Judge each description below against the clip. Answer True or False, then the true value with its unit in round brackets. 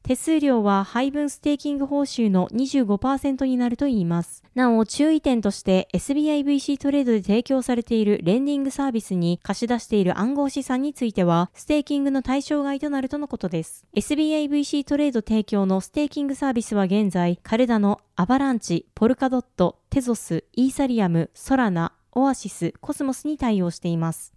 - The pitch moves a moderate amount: False (5.8 semitones)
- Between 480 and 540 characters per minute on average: False (400 characters per minute)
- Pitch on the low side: False (245 Hz)